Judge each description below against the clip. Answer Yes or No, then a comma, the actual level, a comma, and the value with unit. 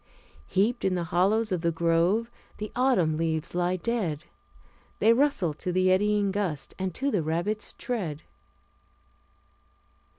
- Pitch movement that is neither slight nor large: Yes, average, 4.2 semitones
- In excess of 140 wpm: No, slow, 135 wpm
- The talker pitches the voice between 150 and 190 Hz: Yes, medium, 185 Hz